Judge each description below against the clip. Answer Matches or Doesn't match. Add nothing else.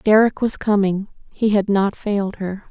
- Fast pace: Doesn't match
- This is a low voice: Doesn't match